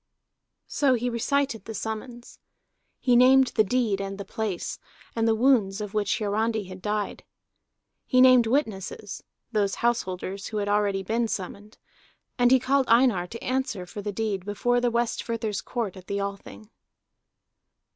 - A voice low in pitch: No, high, 220 Hz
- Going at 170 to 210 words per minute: No, average, 155 wpm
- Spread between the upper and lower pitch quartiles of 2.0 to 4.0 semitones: Yes, average, 3.3 semitones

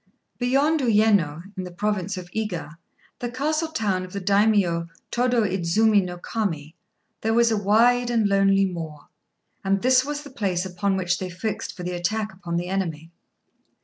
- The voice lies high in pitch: Yes, high, 200 Hz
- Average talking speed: Yes, average, 170 wpm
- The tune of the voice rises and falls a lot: No, average, 4.0 semitones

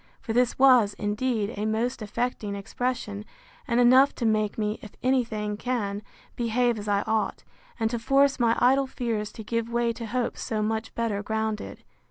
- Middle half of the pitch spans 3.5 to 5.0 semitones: No, narrow, 2.6 semitones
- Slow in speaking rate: No, average, 180 wpm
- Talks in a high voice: Yes, high, 225 Hz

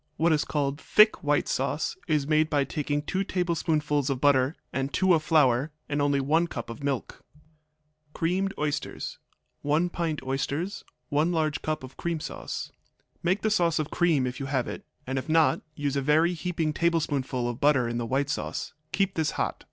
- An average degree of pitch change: Yes, average, 3.1 semitones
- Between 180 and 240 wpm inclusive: Yes, average, 185 wpm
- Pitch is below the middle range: No, medium, 150 Hz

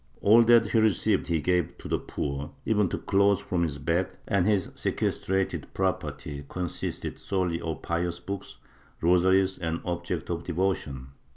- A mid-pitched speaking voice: No, very low, 90 Hz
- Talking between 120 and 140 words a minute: No, average, 160 wpm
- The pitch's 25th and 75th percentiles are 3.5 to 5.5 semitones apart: No, average, 2.7 semitones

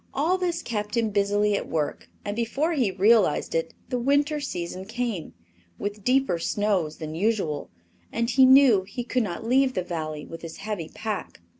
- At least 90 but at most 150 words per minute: No, average, 175 wpm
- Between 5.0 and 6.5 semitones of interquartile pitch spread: Yes, wide, 5.5 semitones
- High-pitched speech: Yes, high, 215 Hz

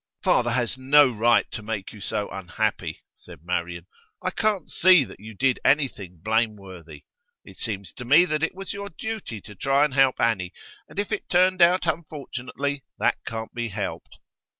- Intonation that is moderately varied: No, wide, 6.7 semitones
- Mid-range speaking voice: No, low, 125 Hz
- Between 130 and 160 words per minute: No, average, 175 wpm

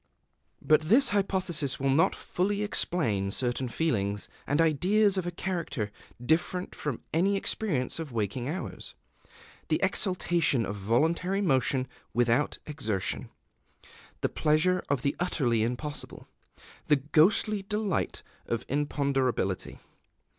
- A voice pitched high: No, medium, 150 Hz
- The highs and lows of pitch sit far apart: Yes, wide, 6.7 semitones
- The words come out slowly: Yes, slow, 115 wpm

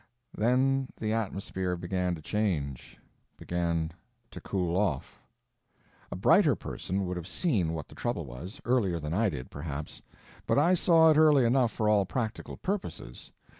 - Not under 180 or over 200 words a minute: No, average, 155 wpm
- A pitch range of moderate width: No, wide, 6.4 semitones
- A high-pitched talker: No, very low, 95 Hz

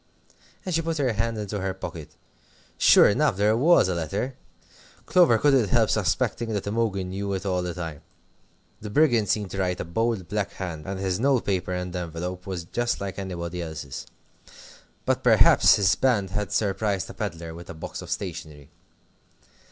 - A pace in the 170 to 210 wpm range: Yes, average, 175 wpm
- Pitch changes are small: No, average, 3.8 semitones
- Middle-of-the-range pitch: No, very low, 95 Hz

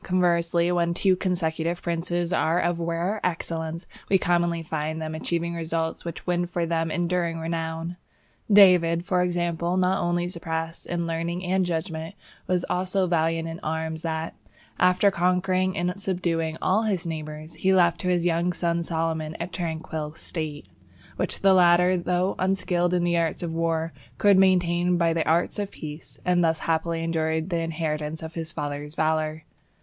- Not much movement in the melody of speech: Yes, narrow, 1.7 semitones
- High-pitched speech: No, medium, 170 Hz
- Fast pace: No, average, 165 wpm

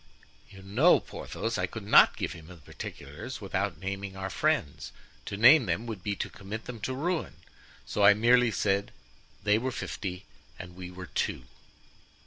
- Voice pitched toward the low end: Yes, low, 100 Hz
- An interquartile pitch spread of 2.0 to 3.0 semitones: No, average, 3.7 semitones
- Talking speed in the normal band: Yes, average, 170 wpm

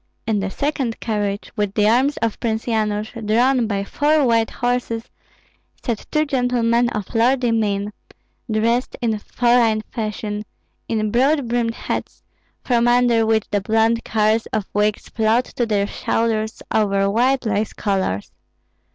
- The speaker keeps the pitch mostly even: Yes, narrow, 2.3 semitones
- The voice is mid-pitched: No, high, 225 Hz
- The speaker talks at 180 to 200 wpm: No, average, 145 wpm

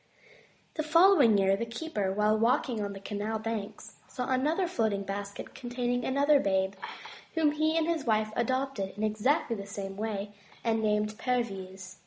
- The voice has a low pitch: No, high, 220 Hz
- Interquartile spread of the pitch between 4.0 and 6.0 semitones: Yes, average, 4.7 semitones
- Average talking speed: Yes, average, 160 wpm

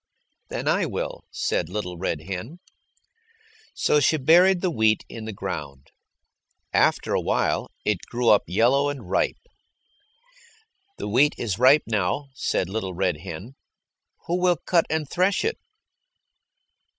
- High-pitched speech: No, low, 115 Hz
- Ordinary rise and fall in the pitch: No, wide, 8.2 semitones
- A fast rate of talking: No, average, 140 wpm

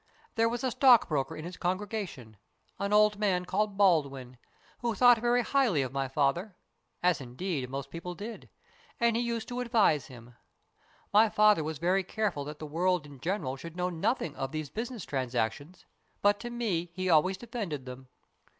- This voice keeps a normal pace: Yes, average, 185 wpm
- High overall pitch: No, medium, 180 Hz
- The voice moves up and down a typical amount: No, wide, 7.1 semitones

